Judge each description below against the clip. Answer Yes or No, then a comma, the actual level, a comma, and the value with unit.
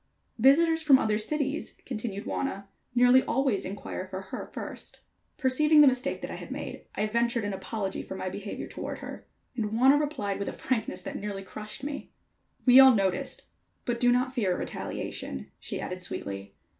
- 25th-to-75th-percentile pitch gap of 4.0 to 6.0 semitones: Yes, average, 5.2 semitones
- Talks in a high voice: Yes, high, 235 Hz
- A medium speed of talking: Yes, average, 180 wpm